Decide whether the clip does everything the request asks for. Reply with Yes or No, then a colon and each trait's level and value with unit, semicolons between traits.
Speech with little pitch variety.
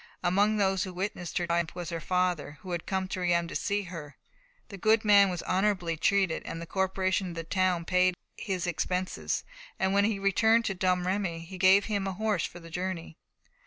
Yes: narrow, 2.2 semitones